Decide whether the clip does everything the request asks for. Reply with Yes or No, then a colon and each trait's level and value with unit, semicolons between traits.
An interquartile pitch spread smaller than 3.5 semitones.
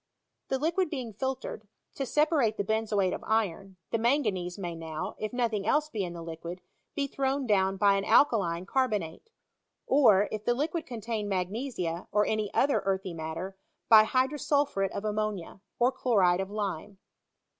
No: average, 5.2 semitones